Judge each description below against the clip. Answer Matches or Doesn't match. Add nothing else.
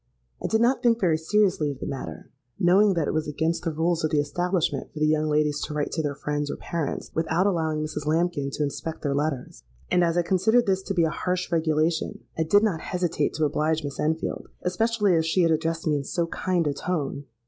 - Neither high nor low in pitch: Matches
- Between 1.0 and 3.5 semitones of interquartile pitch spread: Matches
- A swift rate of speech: Matches